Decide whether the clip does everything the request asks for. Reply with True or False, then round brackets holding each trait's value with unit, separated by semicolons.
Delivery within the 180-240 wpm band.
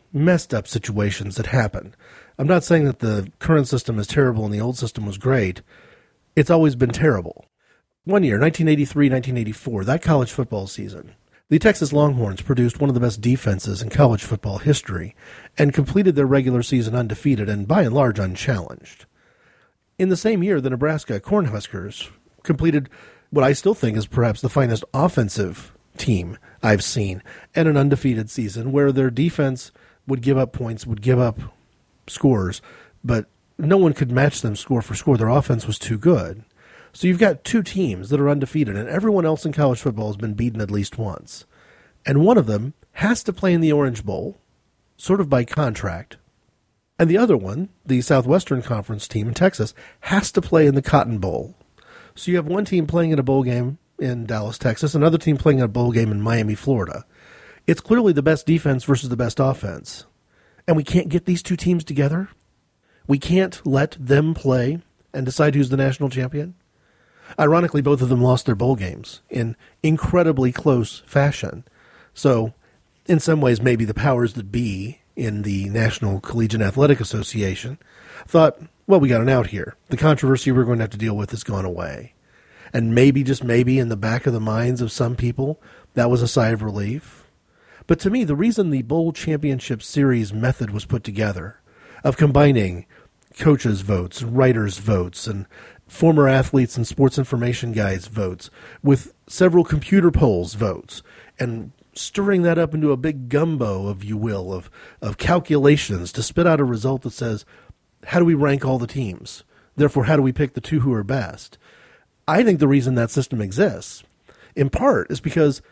True (185 wpm)